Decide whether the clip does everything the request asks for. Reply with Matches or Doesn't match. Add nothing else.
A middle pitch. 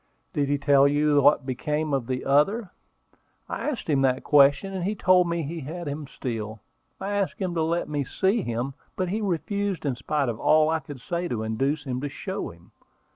Matches